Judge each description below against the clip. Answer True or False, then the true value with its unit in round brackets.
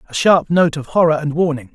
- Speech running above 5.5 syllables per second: True (5.7 syllables/s)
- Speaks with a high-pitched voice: False (155 Hz)